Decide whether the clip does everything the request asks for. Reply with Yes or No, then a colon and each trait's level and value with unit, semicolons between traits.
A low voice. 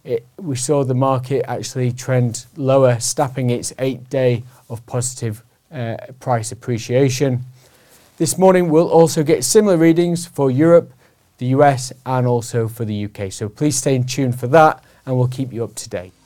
Yes: low, 130 Hz